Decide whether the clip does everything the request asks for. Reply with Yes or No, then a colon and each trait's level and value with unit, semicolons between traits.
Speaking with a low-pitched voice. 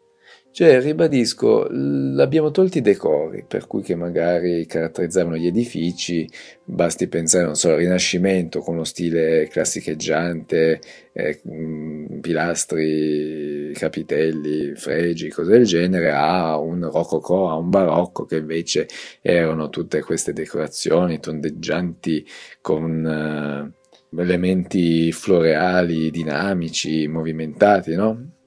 Yes: very low, 85 Hz